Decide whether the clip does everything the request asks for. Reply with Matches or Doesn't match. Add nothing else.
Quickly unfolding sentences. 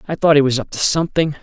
Matches